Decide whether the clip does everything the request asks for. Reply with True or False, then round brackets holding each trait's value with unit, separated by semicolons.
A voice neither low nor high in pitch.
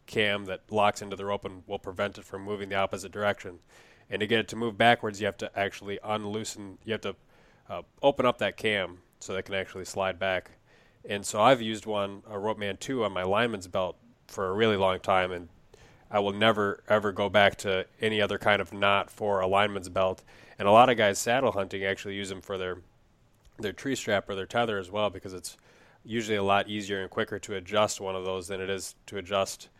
False (100 Hz)